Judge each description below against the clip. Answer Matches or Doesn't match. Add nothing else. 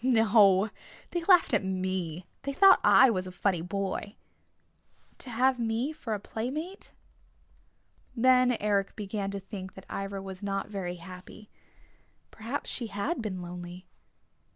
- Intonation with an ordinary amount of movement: Matches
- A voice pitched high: Matches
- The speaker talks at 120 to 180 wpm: Matches